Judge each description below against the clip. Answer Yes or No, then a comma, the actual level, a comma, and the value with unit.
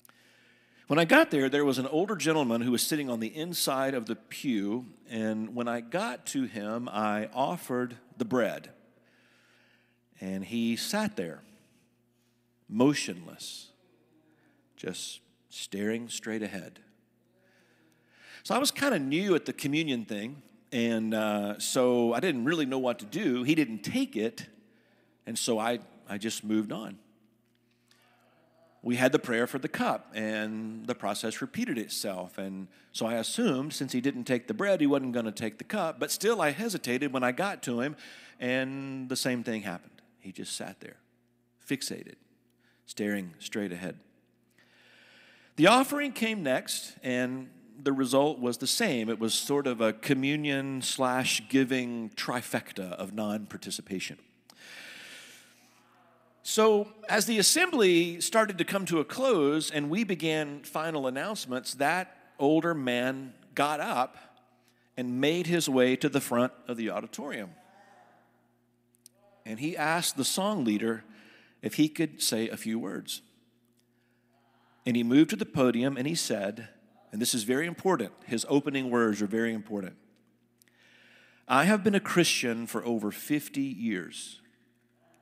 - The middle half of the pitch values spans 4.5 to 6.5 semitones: Yes, average, 5.2 semitones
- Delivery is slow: No, average, 150 wpm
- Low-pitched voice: Yes, low, 125 Hz